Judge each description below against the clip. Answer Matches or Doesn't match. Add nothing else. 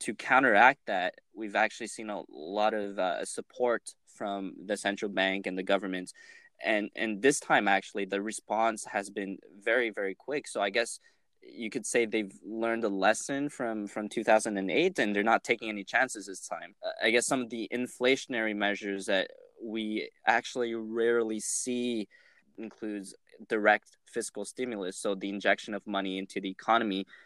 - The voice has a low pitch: Matches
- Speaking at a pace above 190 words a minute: Doesn't match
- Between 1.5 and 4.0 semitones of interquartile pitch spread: Matches